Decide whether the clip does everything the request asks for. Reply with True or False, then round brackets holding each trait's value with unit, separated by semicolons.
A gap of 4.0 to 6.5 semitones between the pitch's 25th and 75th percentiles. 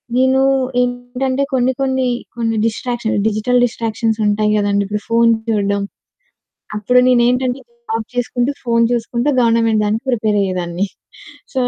False (2.7 semitones)